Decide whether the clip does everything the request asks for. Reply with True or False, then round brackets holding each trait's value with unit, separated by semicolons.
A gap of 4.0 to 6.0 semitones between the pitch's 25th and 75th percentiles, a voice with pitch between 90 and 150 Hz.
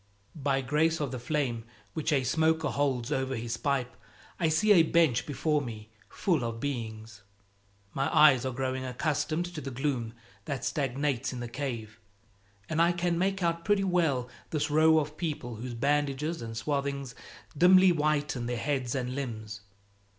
True (4.3 semitones; 140 Hz)